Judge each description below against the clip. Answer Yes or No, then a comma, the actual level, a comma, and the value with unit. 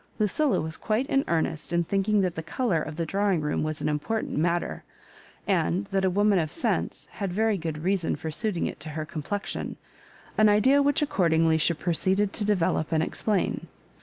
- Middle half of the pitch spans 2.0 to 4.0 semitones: No, average, 4.7 semitones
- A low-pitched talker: No, medium, 180 Hz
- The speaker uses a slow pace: No, average, 195 wpm